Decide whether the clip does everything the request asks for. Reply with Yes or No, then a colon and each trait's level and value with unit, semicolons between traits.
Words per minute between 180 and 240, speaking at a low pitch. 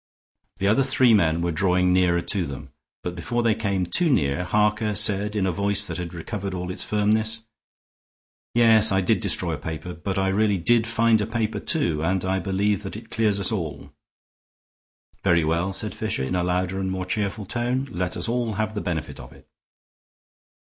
Yes: average, 195 wpm; low, 100 Hz